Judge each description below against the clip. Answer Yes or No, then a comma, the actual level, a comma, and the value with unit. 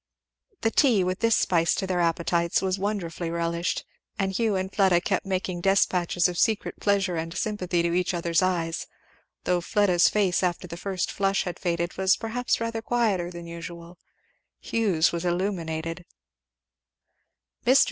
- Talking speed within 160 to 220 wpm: No, average, 150 wpm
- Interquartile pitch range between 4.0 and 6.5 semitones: No, narrow, 2.5 semitones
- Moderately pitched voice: Yes, medium, 180 Hz